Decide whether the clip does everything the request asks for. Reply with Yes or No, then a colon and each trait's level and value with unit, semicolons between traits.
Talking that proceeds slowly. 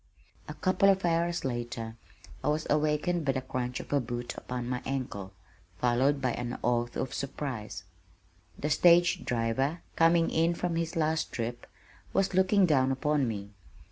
No: average, 160 wpm